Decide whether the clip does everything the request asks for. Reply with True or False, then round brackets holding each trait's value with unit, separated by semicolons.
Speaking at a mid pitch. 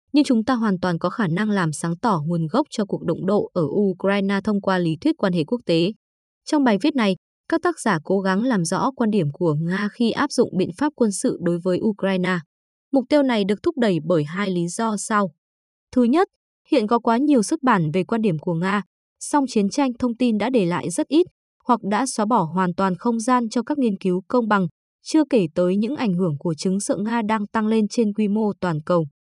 False (210 Hz)